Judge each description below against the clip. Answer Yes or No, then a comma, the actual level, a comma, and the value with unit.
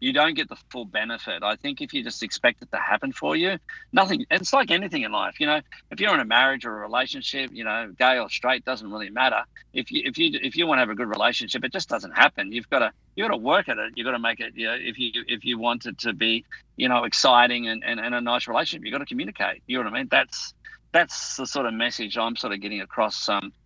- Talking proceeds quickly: Yes, fast, 285 wpm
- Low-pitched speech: Yes, low, 120 Hz